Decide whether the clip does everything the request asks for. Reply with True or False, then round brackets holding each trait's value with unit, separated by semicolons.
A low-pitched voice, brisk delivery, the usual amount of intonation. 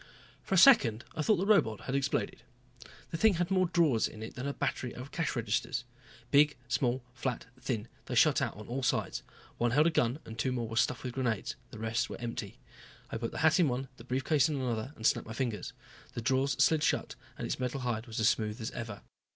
True (125 Hz; 230 wpm; 4.0 semitones)